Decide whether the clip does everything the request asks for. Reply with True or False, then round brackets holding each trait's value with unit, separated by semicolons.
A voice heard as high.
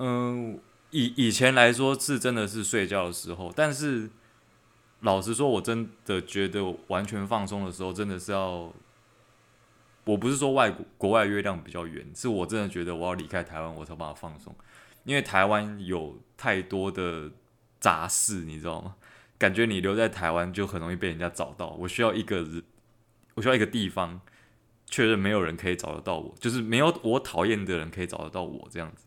False (100 Hz)